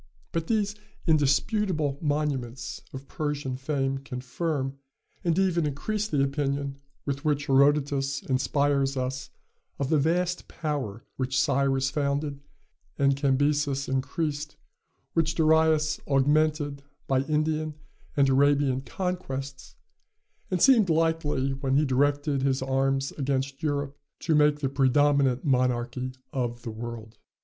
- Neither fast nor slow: No, slow, 120 wpm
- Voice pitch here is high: No, medium, 140 Hz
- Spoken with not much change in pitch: Yes, narrow, 2.3 semitones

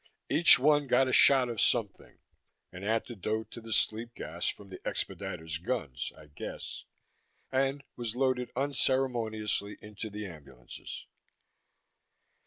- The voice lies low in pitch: Yes, low, 115 Hz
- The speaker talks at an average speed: No, slow, 125 wpm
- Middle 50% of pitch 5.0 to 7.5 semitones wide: No, average, 4.6 semitones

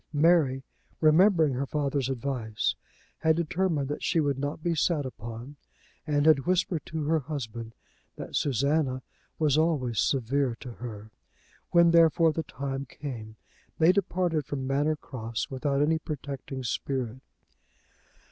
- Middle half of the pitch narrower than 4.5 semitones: Yes, average, 3.7 semitones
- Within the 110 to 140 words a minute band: Yes, slow, 135 wpm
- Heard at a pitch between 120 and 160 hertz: Yes, medium, 140 Hz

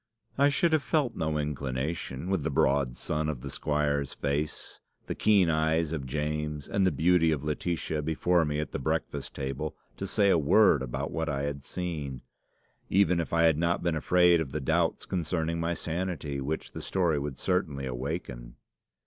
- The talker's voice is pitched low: Yes, very low, 80 Hz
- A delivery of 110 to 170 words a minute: No, average, 180 wpm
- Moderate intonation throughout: Yes, average, 3.4 semitones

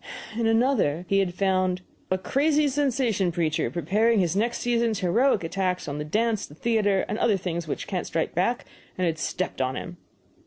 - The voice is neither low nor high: No, high, 195 Hz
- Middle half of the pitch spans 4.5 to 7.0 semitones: Yes, average, 4.9 semitones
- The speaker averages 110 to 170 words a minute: No, average, 185 wpm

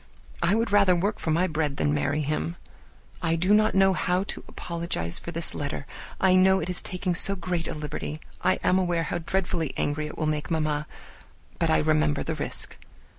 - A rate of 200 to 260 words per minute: Yes, fast, 205 wpm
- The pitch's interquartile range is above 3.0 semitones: Yes, average, 3.4 semitones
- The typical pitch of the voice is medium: Yes, medium, 170 Hz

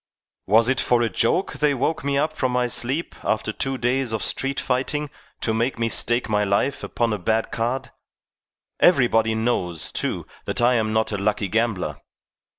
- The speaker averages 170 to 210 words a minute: Yes, average, 180 wpm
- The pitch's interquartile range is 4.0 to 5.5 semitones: No, average, 3.2 semitones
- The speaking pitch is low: Yes, low, 120 Hz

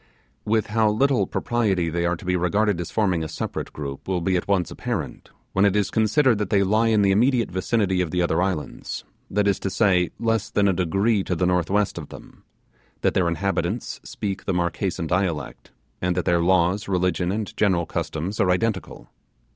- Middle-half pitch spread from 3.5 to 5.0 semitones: No, average, 3.0 semitones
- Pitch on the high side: No, very low, 95 Hz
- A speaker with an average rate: Yes, average, 195 wpm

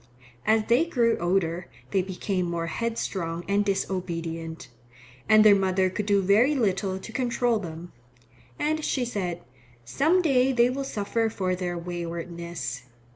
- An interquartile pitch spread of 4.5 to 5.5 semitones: Yes, average, 5.0 semitones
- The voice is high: Yes, high, 195 Hz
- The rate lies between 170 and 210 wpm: No, average, 140 wpm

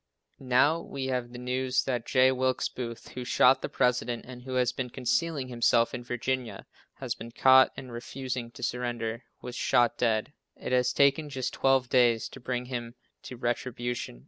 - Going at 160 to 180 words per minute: Yes, average, 175 wpm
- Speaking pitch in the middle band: No, low, 125 Hz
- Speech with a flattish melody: Yes, narrow, 1.3 semitones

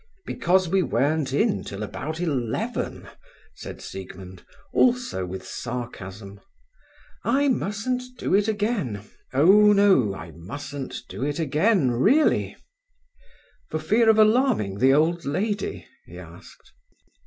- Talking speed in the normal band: No, slow, 120 wpm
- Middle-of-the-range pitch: Yes, medium, 155 Hz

